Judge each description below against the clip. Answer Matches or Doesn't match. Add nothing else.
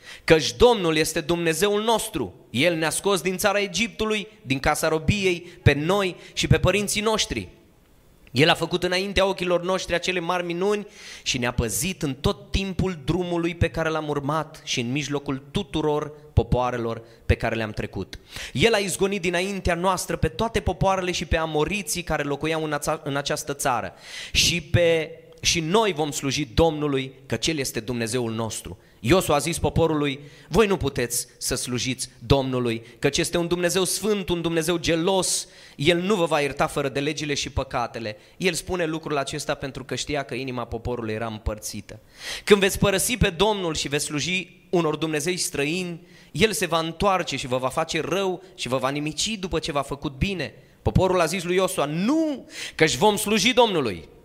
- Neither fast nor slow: Doesn't match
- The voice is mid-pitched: Matches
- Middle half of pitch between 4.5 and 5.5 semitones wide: Matches